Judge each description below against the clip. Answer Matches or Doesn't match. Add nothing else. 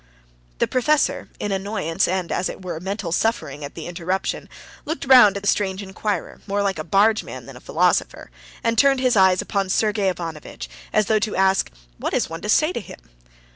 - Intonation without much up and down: Doesn't match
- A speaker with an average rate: Matches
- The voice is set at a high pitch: Matches